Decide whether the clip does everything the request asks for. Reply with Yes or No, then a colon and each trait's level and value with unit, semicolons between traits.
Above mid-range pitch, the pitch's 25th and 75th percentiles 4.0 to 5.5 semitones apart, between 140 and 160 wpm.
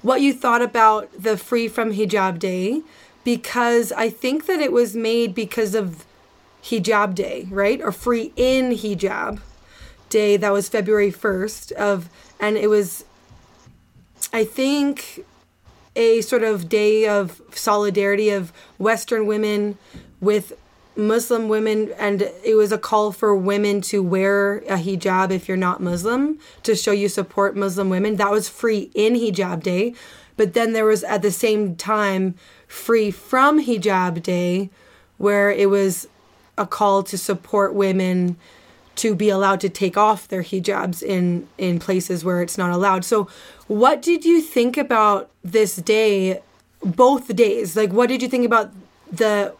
No: high, 210 Hz; narrow, 2.5 semitones; average, 155 wpm